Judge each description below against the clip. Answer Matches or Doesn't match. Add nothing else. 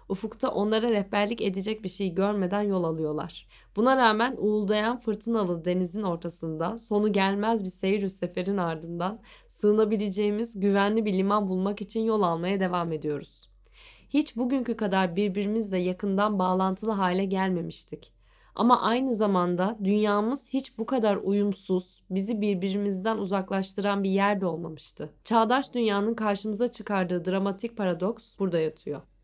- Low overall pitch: Doesn't match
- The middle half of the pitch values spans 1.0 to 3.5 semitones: Matches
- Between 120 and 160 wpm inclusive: Matches